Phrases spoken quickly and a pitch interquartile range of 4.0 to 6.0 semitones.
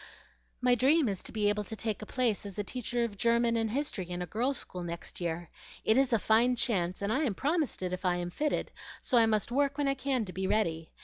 Yes: fast, 250 wpm; average, 5.1 semitones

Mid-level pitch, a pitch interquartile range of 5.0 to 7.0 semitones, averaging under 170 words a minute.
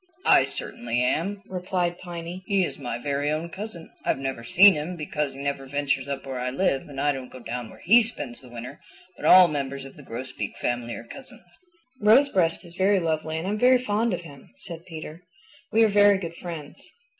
No: medium, 160 Hz; wide, 5.6 semitones; fast, 205 wpm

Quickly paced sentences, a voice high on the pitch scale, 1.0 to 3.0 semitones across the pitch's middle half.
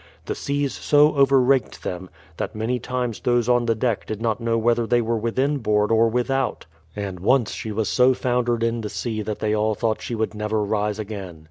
No: fast, 215 wpm; low, 115 Hz; narrow, 2.5 semitones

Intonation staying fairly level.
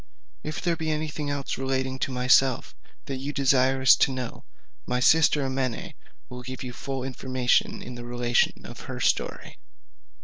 Yes: narrow, 1.7 semitones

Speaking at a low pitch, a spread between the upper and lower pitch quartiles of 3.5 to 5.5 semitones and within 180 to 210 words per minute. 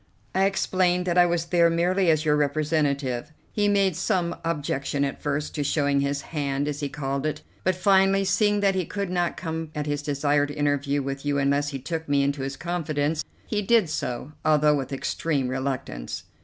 No: medium, 150 Hz; average, 3.8 semitones; average, 190 wpm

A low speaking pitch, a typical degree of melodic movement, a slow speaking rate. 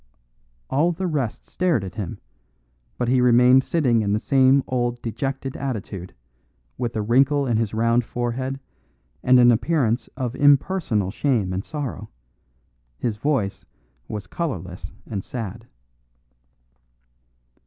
Yes: low, 120 Hz; average, 3.8 semitones; slow, 125 wpm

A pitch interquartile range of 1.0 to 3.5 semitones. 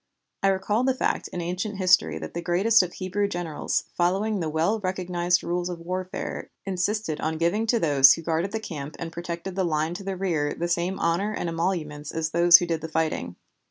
Yes: average, 2.8 semitones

